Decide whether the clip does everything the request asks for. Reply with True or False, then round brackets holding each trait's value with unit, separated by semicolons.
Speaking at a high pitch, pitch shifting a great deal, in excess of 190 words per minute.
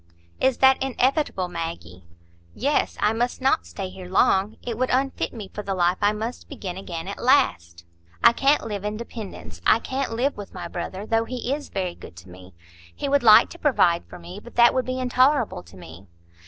True (210 Hz; 6.8 semitones; 200 wpm)